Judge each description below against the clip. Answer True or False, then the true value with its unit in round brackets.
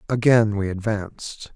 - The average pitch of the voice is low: True (105 Hz)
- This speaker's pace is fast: False (115 wpm)